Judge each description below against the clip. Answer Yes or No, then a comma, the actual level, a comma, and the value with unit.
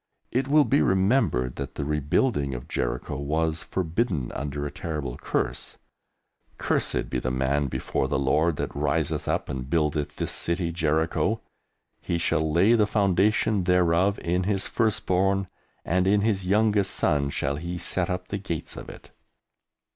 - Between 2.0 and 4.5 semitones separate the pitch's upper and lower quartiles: No, average, 5.2 semitones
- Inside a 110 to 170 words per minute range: Yes, average, 155 wpm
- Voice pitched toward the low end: Yes, very low, 85 Hz